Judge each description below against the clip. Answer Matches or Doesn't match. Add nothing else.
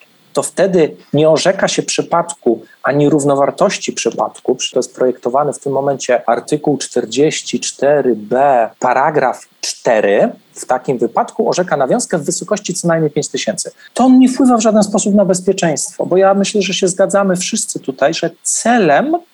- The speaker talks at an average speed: Matches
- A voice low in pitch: Doesn't match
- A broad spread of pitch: Matches